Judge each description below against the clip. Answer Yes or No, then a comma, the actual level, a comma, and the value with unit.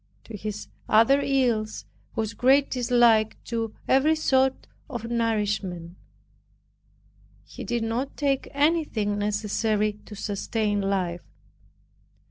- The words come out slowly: Yes, slow, 100 wpm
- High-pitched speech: Yes, high, 225 Hz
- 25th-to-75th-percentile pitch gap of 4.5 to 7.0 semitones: No, average, 3.9 semitones